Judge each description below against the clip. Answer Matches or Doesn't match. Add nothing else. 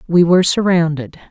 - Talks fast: Doesn't match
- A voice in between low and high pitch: Matches